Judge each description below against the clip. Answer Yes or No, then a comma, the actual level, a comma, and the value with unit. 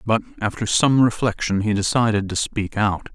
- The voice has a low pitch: Yes, low, 105 Hz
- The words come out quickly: No, average, 170 wpm